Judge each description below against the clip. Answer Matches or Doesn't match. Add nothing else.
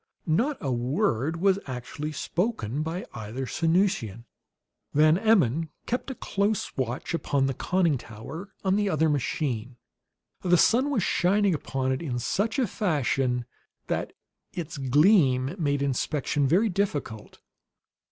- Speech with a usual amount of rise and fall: Doesn't match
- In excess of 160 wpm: Doesn't match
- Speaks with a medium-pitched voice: Matches